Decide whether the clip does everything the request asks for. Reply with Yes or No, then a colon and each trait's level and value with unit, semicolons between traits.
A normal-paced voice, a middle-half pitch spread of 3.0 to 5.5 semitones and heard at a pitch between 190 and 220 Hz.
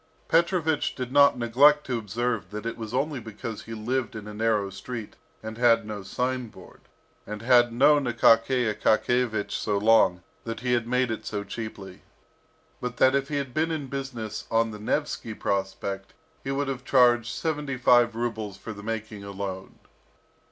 No: average, 170 wpm; average, 3.3 semitones; low, 115 Hz